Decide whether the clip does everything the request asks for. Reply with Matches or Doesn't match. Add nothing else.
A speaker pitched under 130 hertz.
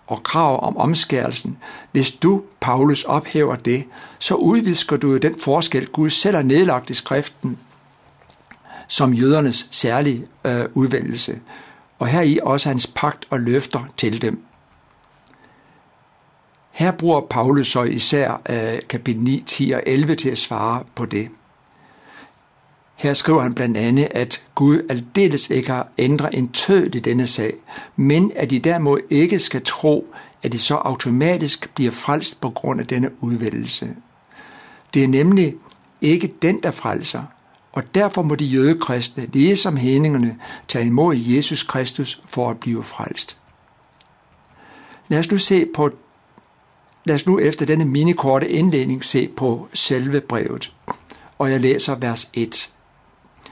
Doesn't match